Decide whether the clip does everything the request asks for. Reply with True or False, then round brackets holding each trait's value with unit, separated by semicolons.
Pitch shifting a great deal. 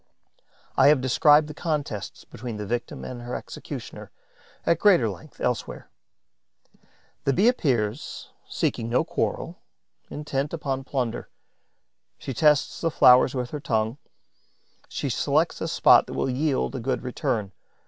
False (3.8 semitones)